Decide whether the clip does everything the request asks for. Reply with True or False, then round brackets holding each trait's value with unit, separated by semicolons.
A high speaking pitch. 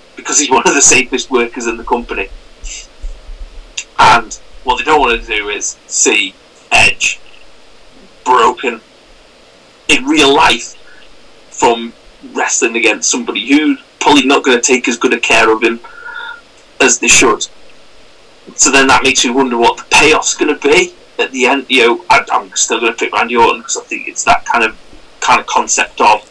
True (350 Hz)